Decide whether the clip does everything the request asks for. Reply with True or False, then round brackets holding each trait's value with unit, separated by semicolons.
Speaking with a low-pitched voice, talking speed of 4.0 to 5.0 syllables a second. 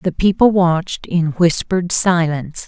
False (175 Hz; 4.6 syllables/s)